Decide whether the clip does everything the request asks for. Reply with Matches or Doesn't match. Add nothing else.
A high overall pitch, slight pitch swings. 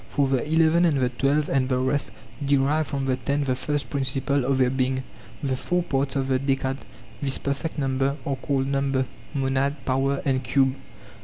Doesn't match